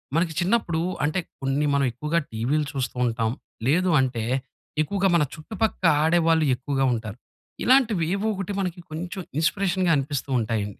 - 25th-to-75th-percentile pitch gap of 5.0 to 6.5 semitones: Yes, wide, 5.5 semitones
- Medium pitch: Yes, medium, 155 Hz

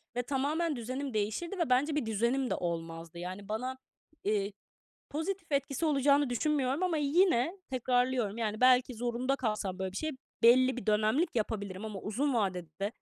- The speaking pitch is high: Yes, high, 245 Hz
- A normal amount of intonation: Yes, average, 5.0 semitones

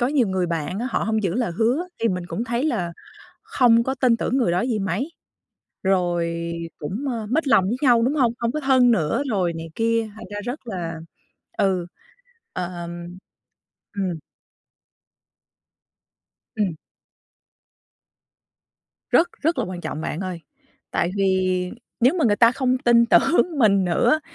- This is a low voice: No, high, 220 Hz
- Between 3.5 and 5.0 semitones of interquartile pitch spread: No, wide, 5.4 semitones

